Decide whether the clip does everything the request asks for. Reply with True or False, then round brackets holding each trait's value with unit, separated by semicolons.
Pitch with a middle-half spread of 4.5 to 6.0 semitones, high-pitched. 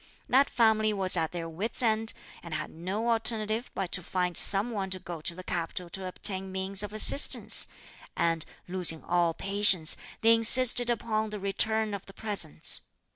False (3.6 semitones; 195 Hz)